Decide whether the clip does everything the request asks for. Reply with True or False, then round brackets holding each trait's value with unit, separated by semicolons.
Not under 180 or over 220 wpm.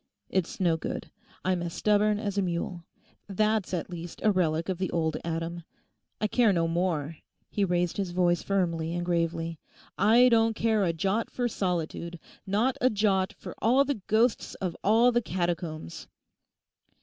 False (160 wpm)